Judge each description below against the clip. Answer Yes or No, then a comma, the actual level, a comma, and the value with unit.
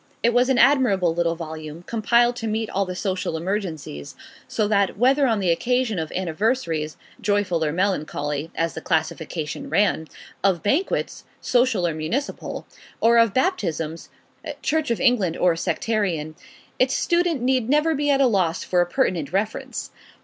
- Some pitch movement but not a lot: No, wide, 6.8 semitones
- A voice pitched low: No, high, 200 Hz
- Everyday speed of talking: Yes, average, 155 wpm